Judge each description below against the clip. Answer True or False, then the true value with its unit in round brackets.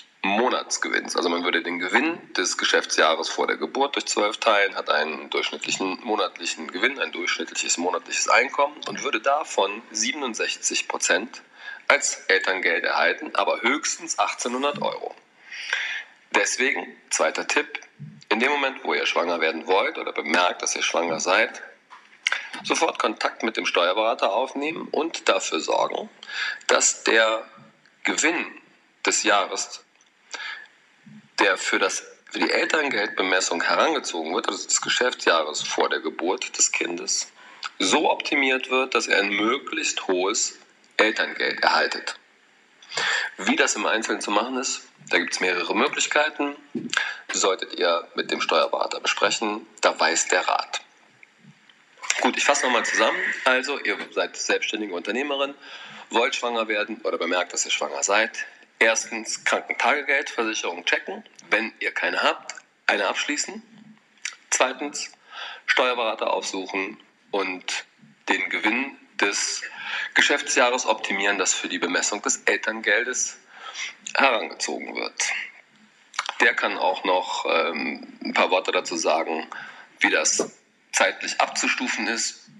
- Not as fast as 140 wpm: True (125 wpm)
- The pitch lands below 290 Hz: False (380 Hz)